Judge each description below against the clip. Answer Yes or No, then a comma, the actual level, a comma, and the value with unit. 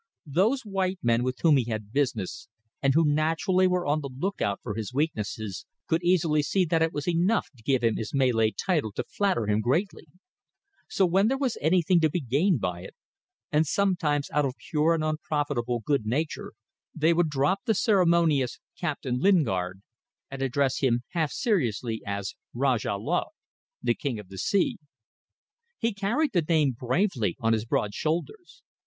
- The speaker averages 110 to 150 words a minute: No, average, 175 wpm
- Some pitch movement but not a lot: No, wide, 6.8 semitones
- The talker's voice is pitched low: No, medium, 150 Hz